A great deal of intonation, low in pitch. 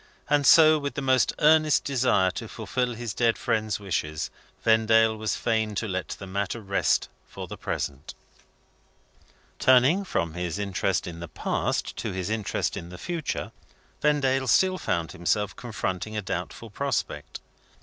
Yes: wide, 5.7 semitones; low, 110 Hz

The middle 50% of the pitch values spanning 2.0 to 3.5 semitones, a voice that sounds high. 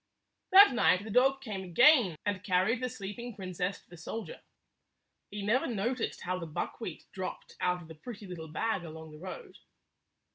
No: average, 4.9 semitones; high, 195 Hz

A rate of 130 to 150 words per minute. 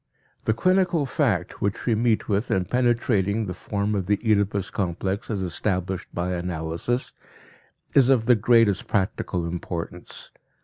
Yes: average, 140 wpm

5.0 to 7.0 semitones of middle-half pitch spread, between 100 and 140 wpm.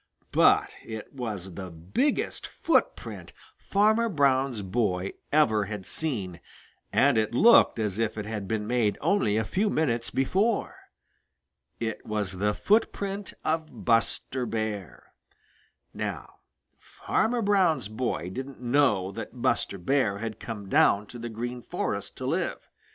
Yes: wide, 5.5 semitones; slow, 135 wpm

